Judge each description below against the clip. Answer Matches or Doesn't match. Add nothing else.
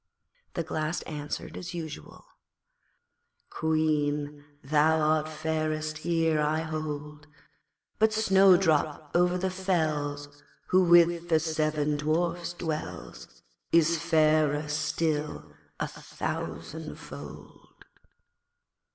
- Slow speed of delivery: Matches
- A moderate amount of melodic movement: Doesn't match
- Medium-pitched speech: Matches